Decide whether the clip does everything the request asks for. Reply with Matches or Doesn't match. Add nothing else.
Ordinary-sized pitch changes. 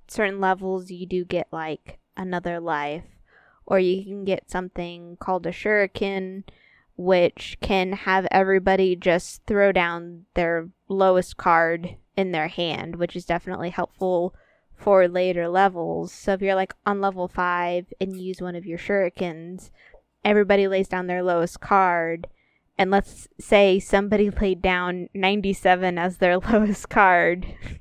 Doesn't match